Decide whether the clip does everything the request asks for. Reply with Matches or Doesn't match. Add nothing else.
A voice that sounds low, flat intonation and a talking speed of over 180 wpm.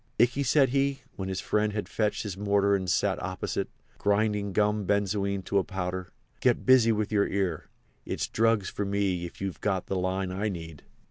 Matches